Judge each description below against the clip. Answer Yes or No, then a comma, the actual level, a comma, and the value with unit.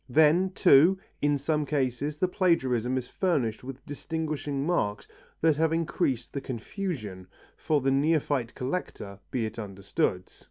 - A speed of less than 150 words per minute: Yes, slow, 135 wpm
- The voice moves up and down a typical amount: Yes, average, 4.7 semitones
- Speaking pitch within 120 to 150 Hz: Yes, medium, 140 Hz